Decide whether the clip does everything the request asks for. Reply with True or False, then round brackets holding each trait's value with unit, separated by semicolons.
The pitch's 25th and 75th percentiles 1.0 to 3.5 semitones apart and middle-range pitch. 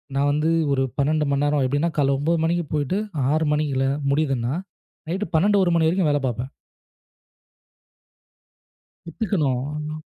True (2.9 semitones; 150 Hz)